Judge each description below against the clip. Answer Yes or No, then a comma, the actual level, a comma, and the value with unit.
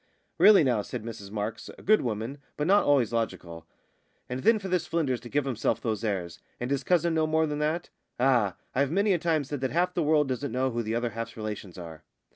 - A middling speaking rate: No, fast, 230 wpm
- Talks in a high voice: No, low, 130 Hz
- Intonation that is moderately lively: No, wide, 5.8 semitones